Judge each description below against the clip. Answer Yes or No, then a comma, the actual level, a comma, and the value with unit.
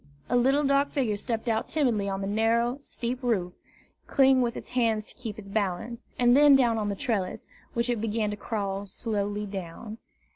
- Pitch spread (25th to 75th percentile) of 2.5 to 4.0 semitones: Yes, average, 3.2 semitones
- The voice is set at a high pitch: Yes, high, 225 Hz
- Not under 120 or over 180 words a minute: No, average, 190 wpm